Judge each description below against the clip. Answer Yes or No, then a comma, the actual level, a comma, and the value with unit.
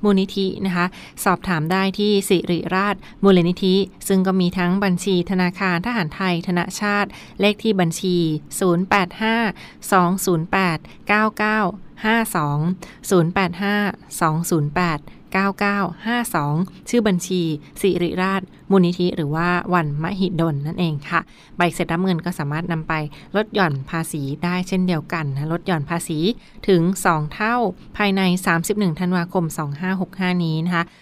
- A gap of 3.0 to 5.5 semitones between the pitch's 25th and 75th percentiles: No, narrow, 2.5 semitones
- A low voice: No, medium, 180 Hz